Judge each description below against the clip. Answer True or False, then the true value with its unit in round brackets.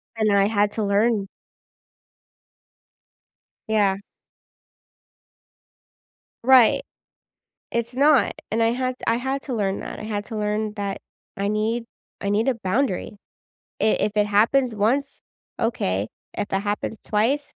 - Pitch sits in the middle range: False (215 Hz)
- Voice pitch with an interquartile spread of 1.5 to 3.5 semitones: True (2.7 semitones)